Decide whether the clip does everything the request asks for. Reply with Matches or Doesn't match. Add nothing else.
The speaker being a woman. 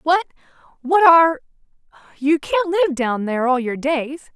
Matches